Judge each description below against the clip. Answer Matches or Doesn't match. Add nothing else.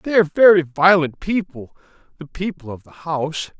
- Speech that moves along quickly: Doesn't match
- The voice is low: Doesn't match